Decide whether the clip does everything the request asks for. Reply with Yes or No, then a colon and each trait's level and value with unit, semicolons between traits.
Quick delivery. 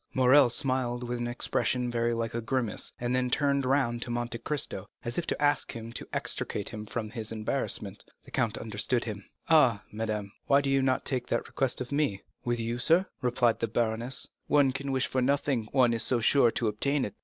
Yes: fast, 215 wpm